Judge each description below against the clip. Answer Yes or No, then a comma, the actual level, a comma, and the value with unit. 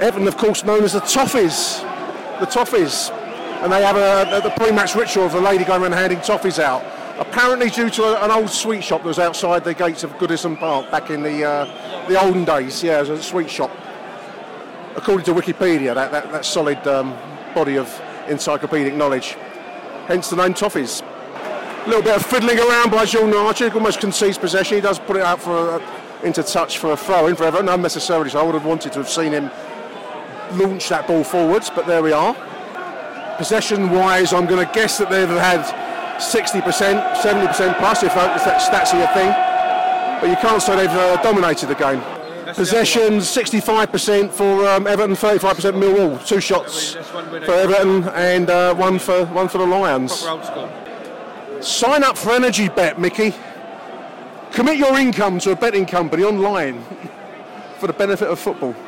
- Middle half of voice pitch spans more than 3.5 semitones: Yes, average, 3.9 semitones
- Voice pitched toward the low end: No, high, 190 Hz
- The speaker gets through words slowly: No, average, 180 wpm